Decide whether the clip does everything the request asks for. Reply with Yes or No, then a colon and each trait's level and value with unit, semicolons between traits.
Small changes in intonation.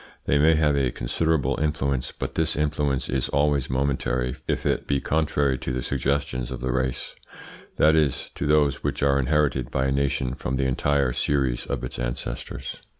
Yes: narrow, 2.2 semitones